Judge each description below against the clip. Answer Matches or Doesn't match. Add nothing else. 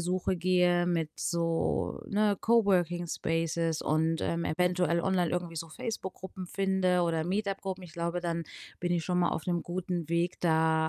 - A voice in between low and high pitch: Matches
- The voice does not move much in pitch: Matches